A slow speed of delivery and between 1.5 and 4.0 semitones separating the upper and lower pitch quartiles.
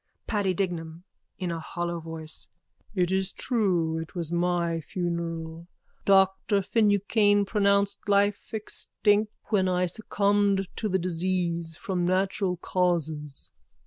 Yes: slow, 120 wpm; average, 2.9 semitones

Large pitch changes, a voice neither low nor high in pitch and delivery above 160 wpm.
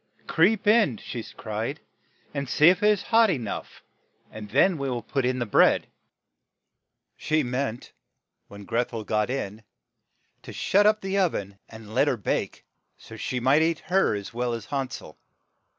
No: wide, 8.0 semitones; low, 130 Hz; average, 180 wpm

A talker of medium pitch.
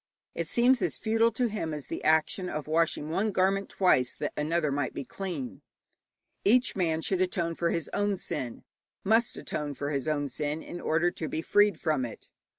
Yes: medium, 165 Hz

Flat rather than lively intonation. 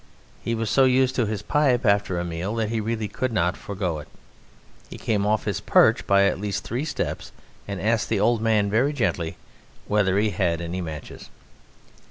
No: average, 3.5 semitones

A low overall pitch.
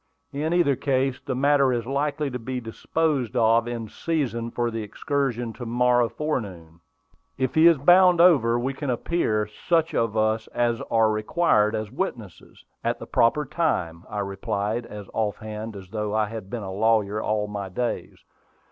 Yes: low, 115 Hz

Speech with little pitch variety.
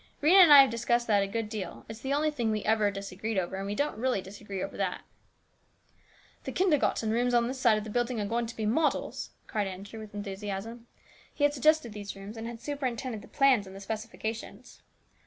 No: average, 3.6 semitones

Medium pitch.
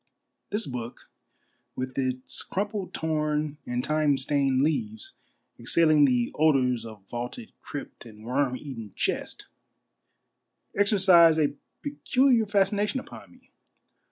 Yes: medium, 150 Hz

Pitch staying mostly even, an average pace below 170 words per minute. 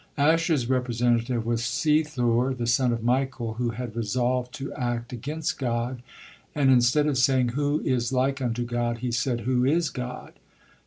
Yes: narrow, 2.2 semitones; average, 160 wpm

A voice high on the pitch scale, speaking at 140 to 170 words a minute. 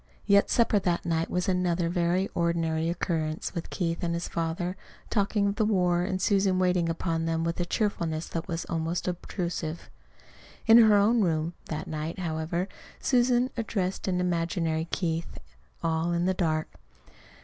No: medium, 175 Hz; average, 160 wpm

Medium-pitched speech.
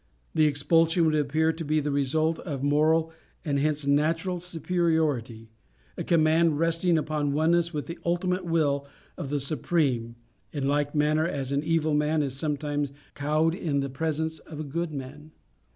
Yes: medium, 155 Hz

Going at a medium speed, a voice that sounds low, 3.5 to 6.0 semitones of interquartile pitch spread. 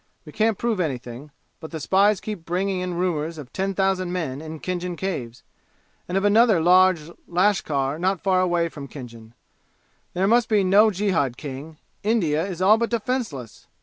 No: average, 170 wpm; medium, 180 Hz; average, 4.4 semitones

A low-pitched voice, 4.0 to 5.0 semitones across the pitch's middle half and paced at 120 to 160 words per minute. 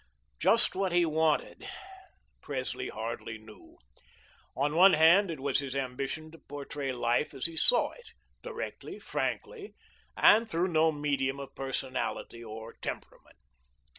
No: medium, 145 Hz; average, 4.4 semitones; slow, 135 wpm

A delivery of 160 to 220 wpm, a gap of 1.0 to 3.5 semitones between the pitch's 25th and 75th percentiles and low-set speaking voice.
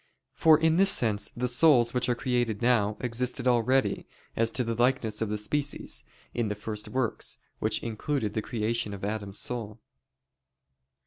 Yes: average, 165 wpm; average, 3.0 semitones; low, 120 Hz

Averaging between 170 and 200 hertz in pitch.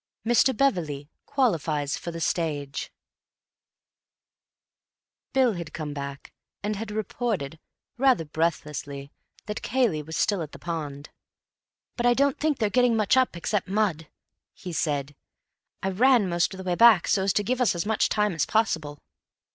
Yes: high, 190 Hz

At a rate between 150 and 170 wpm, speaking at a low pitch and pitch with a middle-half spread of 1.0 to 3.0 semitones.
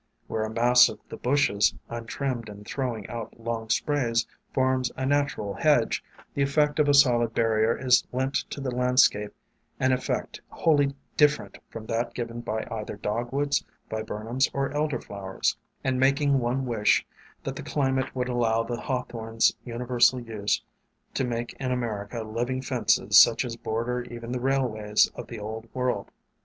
Yes: average, 165 wpm; low, 120 Hz; average, 2.7 semitones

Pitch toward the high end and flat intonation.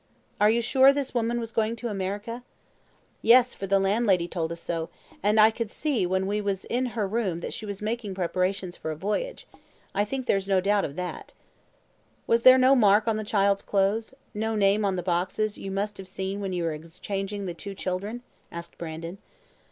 No: high, 200 Hz; average, 3.1 semitones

